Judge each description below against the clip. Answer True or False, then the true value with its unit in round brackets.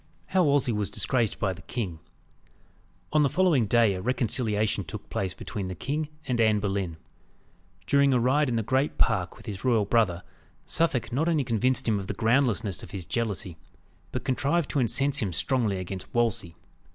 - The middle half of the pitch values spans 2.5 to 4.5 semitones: False (5.1 semitones)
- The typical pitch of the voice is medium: False (115 Hz)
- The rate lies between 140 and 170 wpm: False (185 wpm)